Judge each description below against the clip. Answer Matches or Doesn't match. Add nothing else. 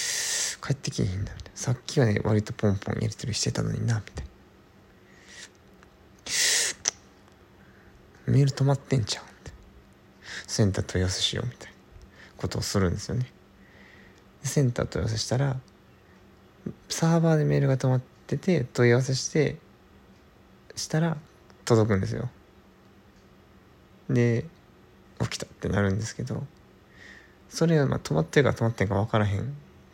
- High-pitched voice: Doesn't match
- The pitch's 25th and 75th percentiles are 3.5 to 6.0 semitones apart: Matches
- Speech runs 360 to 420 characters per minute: Doesn't match